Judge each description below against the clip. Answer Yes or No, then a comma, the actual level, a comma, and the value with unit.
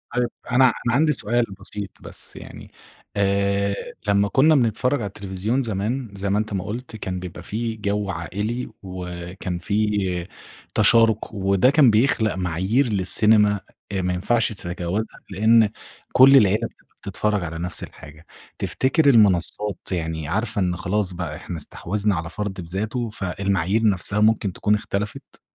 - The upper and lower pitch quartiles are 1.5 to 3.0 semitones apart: No, average, 3.4 semitones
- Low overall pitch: Yes, low, 100 Hz